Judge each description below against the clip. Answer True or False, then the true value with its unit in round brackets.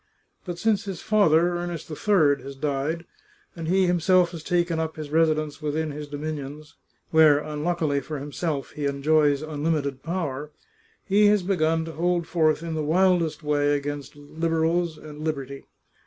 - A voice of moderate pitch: True (155 Hz)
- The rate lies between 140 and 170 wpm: True (165 wpm)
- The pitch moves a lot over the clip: False (2.8 semitones)